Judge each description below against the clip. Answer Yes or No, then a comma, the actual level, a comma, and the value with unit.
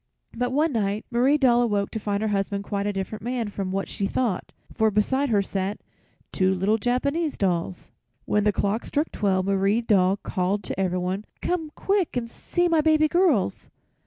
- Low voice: No, high, 210 Hz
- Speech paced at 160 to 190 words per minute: Yes, average, 185 wpm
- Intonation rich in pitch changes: No, average, 4.6 semitones